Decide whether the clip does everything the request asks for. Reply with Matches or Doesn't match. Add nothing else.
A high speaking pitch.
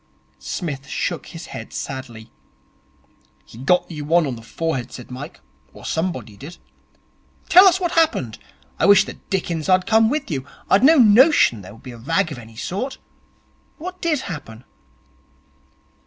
Doesn't match